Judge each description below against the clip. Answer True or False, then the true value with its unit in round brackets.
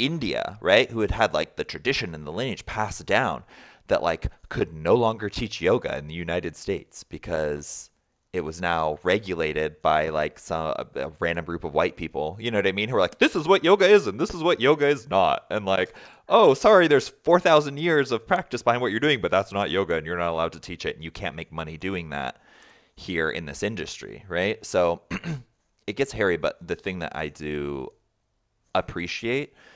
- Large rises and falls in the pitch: True (6.1 semitones)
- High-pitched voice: False (100 Hz)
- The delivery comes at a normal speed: False (215 wpm)